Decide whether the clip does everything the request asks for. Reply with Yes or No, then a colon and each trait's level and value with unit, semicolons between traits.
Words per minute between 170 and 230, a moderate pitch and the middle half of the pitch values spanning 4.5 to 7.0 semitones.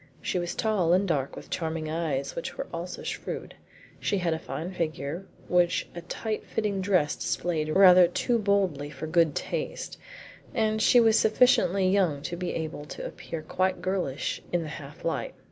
No: average, 175 wpm; medium, 175 Hz; average, 3.6 semitones